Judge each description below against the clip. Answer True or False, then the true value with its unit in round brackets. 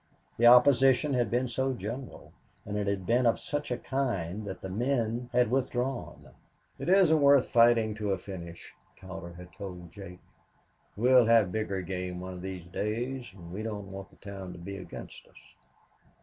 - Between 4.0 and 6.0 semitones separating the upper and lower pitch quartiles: True (4.7 semitones)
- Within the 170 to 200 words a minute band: True (180 wpm)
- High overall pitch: False (110 Hz)